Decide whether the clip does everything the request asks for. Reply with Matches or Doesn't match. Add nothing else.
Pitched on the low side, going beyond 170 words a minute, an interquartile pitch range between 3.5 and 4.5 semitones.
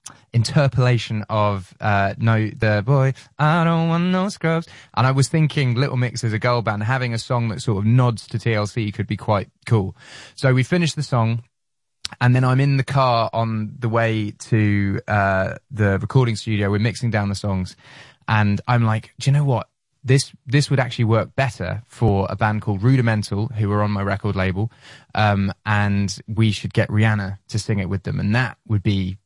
Matches